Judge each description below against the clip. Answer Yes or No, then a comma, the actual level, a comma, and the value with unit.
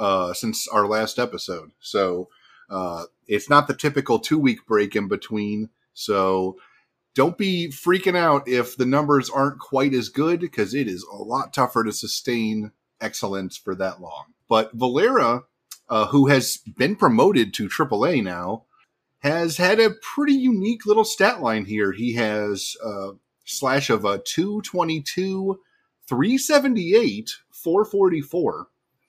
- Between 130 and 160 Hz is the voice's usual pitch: Yes, medium, 140 Hz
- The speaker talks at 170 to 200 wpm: No, average, 140 wpm